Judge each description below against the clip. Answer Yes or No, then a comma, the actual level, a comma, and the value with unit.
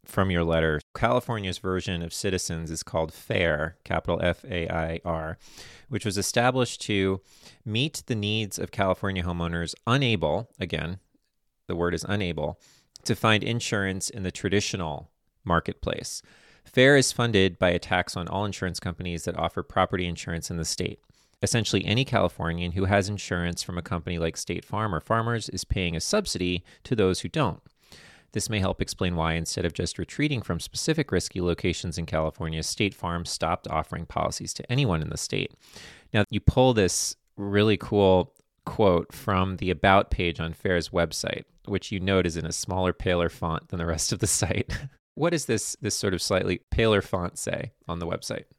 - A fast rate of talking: No, average, 180 wpm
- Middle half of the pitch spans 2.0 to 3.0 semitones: No, average, 3.7 semitones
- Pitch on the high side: No, very low, 95 Hz